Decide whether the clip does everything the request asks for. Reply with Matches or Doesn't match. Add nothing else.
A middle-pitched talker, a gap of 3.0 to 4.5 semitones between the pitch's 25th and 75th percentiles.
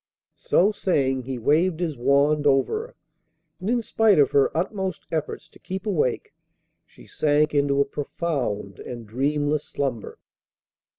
Doesn't match